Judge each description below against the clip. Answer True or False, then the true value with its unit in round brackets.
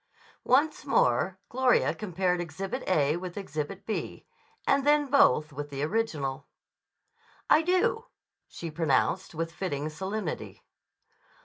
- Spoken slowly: True (115 wpm)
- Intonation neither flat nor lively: False (7.0 semitones)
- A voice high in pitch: False (180 Hz)